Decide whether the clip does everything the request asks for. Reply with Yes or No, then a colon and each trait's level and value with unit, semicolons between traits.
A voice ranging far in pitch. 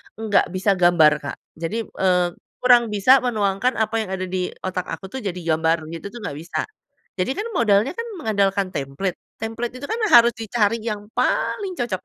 No: average, 4.2 semitones